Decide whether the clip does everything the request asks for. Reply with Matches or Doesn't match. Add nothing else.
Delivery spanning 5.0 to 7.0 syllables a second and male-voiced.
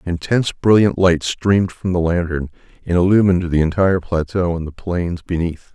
Matches